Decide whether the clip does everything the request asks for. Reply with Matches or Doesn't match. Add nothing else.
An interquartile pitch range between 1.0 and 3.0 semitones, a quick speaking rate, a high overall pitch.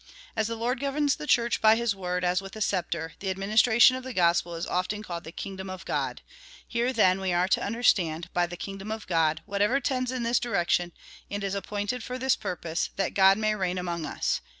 Doesn't match